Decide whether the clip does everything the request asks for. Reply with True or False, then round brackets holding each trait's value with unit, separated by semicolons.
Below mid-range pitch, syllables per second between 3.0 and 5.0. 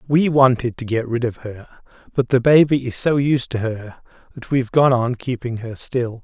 True (125 Hz; 4.9 syllables/s)